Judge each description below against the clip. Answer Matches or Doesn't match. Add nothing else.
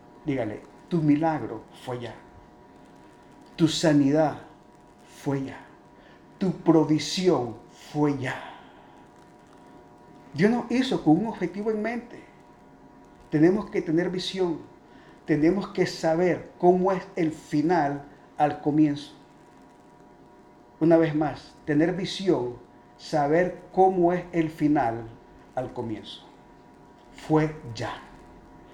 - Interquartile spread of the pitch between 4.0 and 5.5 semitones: Matches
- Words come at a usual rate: Doesn't match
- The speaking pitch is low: Doesn't match